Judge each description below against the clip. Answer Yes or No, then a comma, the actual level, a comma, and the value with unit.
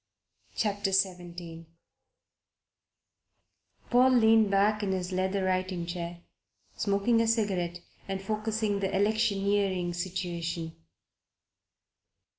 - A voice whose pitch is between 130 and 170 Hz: No, high, 195 Hz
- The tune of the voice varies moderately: Yes, average, 3.0 semitones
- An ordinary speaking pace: No, slow, 85 wpm